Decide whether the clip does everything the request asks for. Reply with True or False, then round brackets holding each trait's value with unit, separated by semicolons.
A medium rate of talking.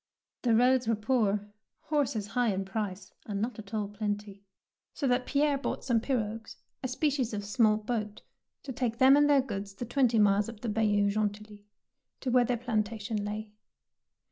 True (175 wpm)